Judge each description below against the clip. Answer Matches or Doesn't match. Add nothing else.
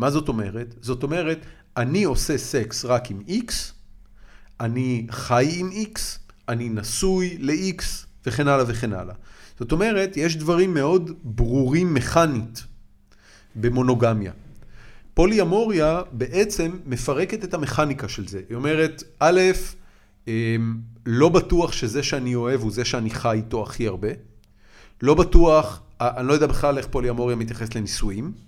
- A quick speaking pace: Doesn't match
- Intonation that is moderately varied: Doesn't match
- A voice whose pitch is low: Matches